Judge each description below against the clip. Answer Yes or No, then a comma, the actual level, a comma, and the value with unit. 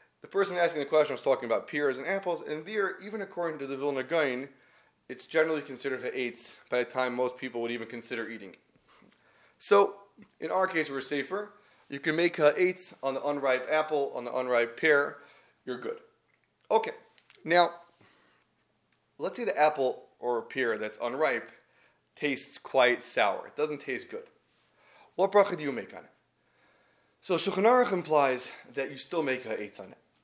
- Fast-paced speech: No, average, 180 wpm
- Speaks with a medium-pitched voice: Yes, medium, 155 Hz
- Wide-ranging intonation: Yes, wide, 6.7 semitones